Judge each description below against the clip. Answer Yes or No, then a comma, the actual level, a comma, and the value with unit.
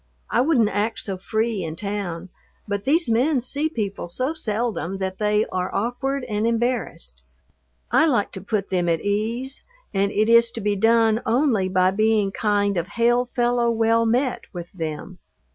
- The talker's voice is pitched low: No, high, 220 Hz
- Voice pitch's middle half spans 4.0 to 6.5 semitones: No, average, 3.5 semitones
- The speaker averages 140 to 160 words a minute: No, average, 170 wpm